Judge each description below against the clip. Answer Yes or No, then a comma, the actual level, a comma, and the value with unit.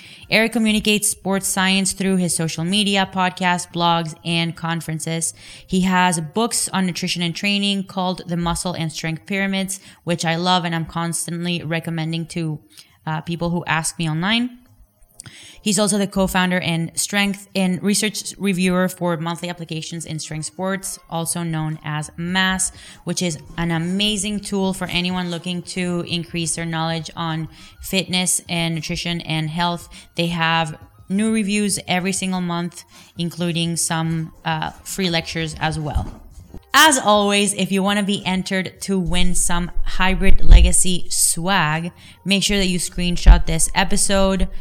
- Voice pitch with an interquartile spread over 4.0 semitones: No, narrow, 2.5 semitones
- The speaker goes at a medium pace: Yes, average, 150 wpm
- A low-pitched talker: No, medium, 175 Hz